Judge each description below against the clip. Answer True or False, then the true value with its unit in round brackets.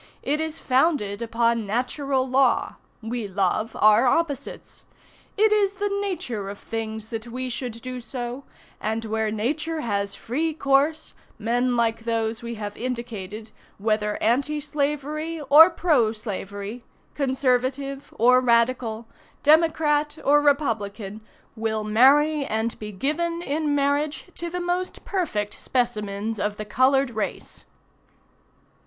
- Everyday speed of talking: False (125 wpm)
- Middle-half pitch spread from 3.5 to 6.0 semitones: True (5.0 semitones)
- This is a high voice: True (250 Hz)